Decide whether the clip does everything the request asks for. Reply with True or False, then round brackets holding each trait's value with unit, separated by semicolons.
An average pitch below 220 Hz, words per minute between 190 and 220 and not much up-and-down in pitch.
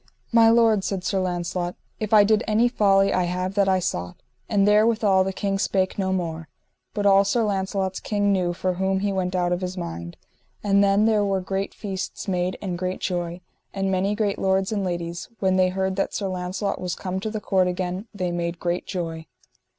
True (190 Hz; 205 wpm; 1.9 semitones)